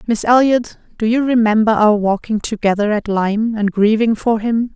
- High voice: Yes, high, 220 Hz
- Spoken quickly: No, average, 175 wpm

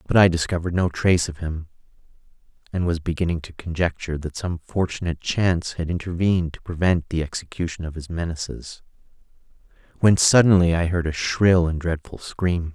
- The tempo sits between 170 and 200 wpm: No, average, 160 wpm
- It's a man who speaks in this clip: Yes, male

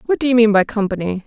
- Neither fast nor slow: No, fast, 285 wpm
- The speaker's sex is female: Yes, female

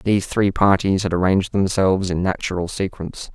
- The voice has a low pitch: Yes, very low, 95 Hz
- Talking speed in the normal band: Yes, average, 160 wpm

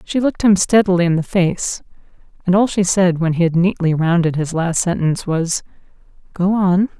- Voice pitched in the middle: Yes, medium, 180 Hz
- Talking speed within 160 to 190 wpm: Yes, average, 180 wpm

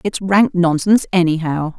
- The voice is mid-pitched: Yes, medium, 175 Hz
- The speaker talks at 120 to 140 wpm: Yes, slow, 135 wpm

